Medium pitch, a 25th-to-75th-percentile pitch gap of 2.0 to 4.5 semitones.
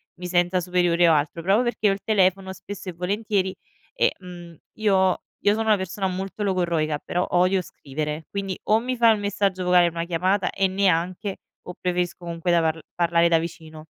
Yes: medium, 180 Hz; narrow, 2.5 semitones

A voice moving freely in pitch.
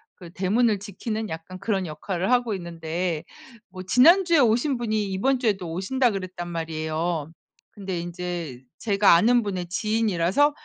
No: average, 4.7 semitones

